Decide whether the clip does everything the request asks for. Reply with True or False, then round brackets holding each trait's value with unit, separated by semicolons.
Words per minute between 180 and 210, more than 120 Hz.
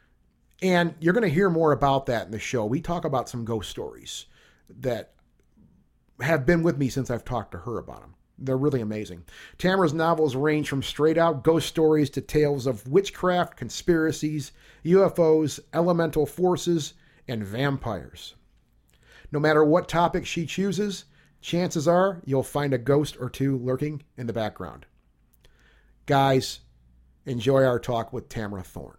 False (155 wpm; 140 Hz)